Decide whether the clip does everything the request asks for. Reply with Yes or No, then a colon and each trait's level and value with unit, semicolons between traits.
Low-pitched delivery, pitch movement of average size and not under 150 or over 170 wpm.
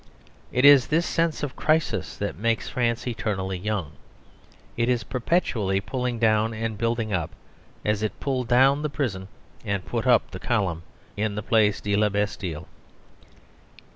Yes: low, 115 Hz; average, 3.7 semitones; average, 155 wpm